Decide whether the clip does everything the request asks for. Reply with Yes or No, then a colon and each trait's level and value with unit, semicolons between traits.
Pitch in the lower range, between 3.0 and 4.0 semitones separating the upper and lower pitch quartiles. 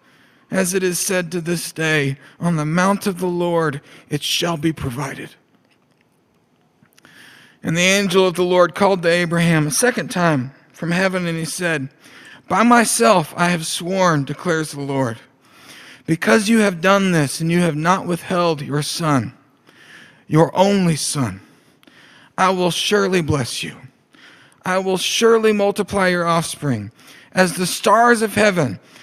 No: medium, 175 Hz; average, 3.3 semitones